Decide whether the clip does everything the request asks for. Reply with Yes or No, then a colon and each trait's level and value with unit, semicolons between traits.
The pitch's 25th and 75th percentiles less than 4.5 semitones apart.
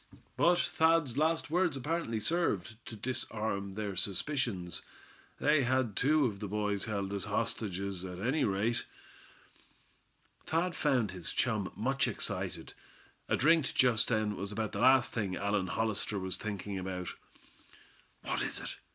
No: wide, 5.4 semitones